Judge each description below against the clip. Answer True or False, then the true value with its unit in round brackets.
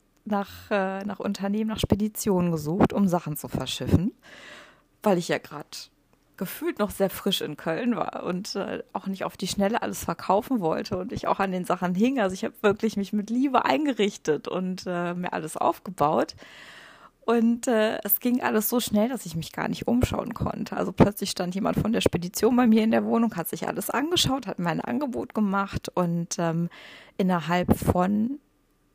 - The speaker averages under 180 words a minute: False (185 wpm)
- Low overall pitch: False (200 Hz)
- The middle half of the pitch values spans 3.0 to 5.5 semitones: True (3.6 semitones)